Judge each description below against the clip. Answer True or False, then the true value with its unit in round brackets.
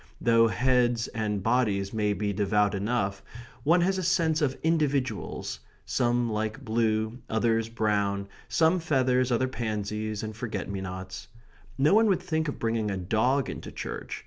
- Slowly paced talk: False (155 wpm)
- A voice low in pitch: True (115 Hz)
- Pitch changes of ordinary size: True (4.1 semitones)